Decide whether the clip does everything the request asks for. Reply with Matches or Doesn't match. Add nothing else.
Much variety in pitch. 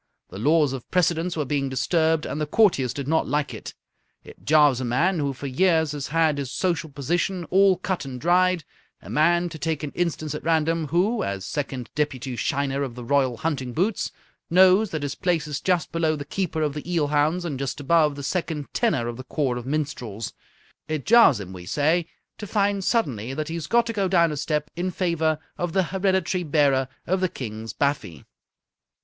Doesn't match